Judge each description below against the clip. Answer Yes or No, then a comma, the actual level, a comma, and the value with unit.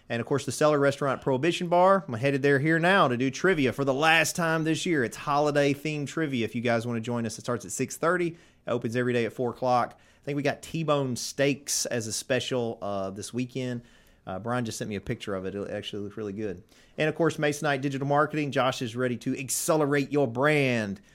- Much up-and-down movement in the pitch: No, average, 3.8 semitones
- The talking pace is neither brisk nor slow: No, fast, 240 wpm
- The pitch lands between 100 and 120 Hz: No, low, 135 Hz